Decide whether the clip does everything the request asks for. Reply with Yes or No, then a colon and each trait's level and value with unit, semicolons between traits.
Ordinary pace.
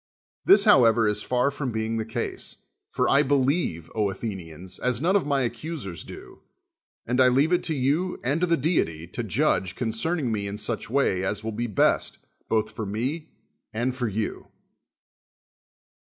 Yes: average, 175 wpm